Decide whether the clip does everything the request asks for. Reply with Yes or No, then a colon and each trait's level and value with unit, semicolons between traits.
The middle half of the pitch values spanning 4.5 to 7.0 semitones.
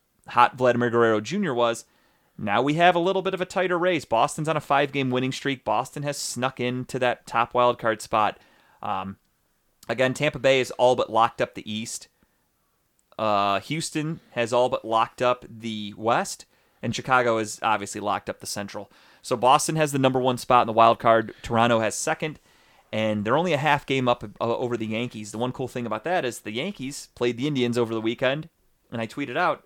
No: average, 3.7 semitones